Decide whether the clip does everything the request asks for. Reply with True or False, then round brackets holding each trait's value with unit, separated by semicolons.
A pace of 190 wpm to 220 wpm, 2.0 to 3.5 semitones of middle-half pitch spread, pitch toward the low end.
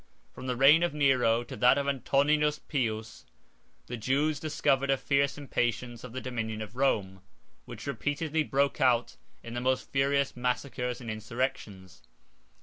False (150 wpm; 2.9 semitones; 130 Hz)